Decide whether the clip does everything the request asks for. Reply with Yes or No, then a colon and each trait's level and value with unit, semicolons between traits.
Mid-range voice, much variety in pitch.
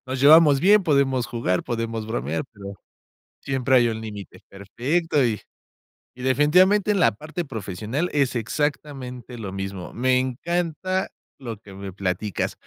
No: low, 125 Hz; wide, 5.7 semitones